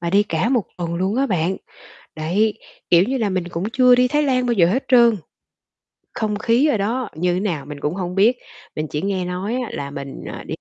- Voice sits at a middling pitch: No, high, 200 Hz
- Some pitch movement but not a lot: No, wide, 5.7 semitones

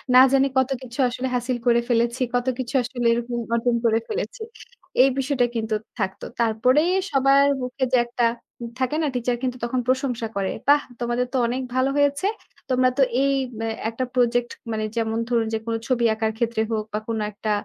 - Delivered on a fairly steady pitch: Yes, narrow, 2.2 semitones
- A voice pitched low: No, high, 245 Hz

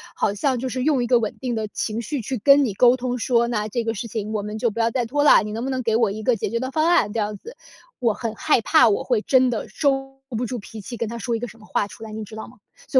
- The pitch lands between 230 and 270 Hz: Yes, high, 235 Hz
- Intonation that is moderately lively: Yes, average, 3.0 semitones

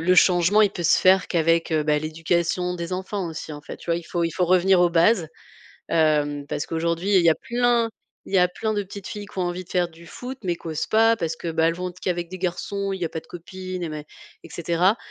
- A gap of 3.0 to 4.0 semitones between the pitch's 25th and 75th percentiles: No, narrow, 2.4 semitones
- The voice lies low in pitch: No, medium, 175 Hz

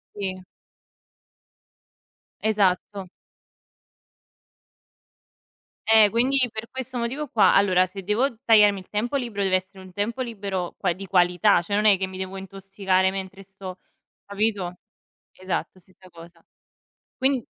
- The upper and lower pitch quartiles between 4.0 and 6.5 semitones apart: No, average, 2.7 semitones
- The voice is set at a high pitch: Yes, high, 195 Hz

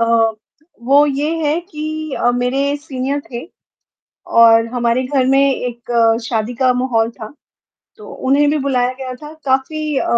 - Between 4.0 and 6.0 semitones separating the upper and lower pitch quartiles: No, average, 3.3 semitones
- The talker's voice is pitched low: No, very high, 260 Hz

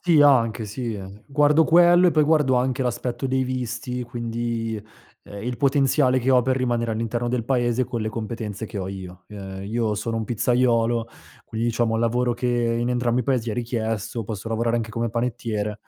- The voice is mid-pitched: No, low, 120 Hz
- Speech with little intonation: Yes, narrow, 2.1 semitones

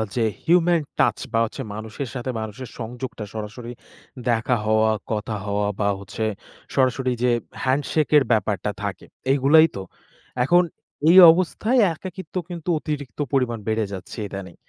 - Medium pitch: No, low, 125 Hz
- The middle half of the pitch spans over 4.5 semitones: Yes, wide, 5.4 semitones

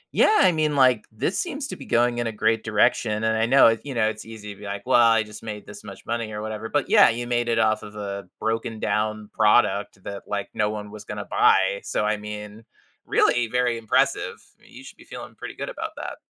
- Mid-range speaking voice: No, low, 110 Hz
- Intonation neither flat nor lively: No, narrow, 2.1 semitones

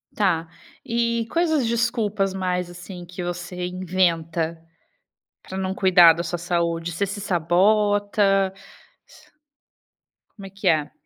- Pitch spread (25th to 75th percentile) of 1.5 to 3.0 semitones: Yes, average, 2.7 semitones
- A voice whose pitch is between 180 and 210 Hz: Yes, medium, 185 Hz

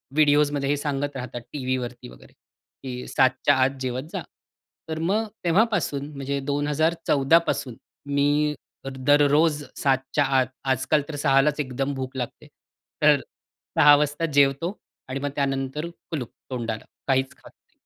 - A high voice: No, medium, 140 Hz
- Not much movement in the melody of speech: Yes, narrow, 2.0 semitones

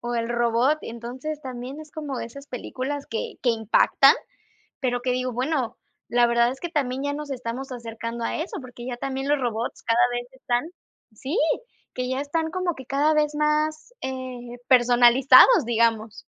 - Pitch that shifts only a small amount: No, average, 3.2 semitones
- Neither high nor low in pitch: No, very high, 255 Hz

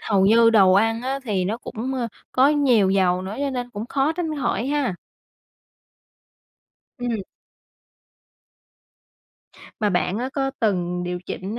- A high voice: Yes, high, 225 Hz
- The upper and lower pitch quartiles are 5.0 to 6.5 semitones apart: Yes, average, 5.3 semitones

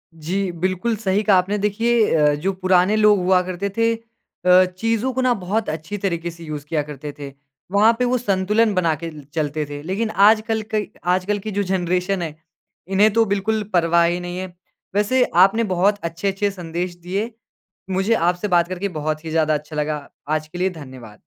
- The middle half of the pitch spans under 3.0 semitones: No, average, 4.0 semitones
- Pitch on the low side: No, medium, 185 Hz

